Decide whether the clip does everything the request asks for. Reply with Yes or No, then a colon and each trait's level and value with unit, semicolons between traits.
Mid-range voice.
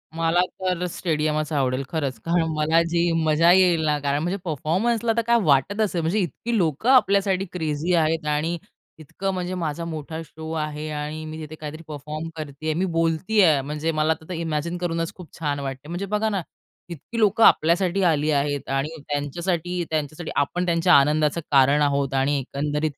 Yes: medium, 160 Hz